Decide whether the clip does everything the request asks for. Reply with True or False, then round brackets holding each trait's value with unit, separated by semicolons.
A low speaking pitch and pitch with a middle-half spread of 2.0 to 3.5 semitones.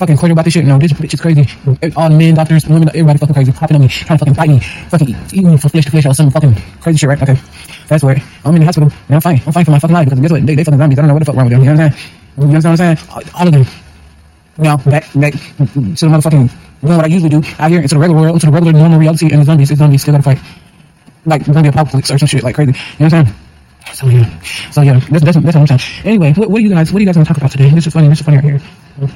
False (150 Hz; 2.6 semitones)